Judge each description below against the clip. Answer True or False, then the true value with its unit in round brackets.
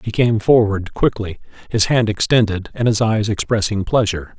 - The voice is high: False (110 Hz)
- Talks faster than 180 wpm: False (165 wpm)